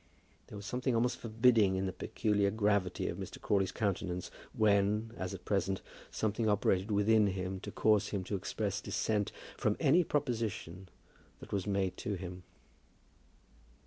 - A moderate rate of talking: Yes, average, 150 wpm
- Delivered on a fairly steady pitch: Yes, narrow, 2.3 semitones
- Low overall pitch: Yes, low, 100 Hz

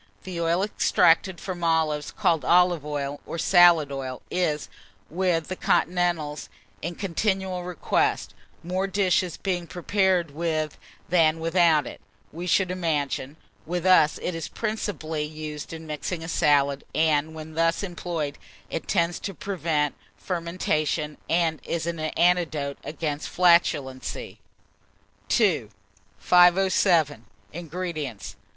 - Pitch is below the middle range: No, medium, 165 Hz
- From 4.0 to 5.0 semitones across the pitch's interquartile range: No, average, 2.8 semitones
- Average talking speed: No, slow, 120 wpm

